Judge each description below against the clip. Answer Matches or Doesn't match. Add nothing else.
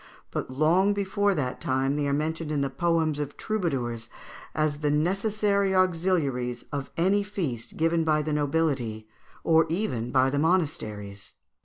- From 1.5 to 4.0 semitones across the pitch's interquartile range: Doesn't match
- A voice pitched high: Doesn't match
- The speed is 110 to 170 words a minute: Matches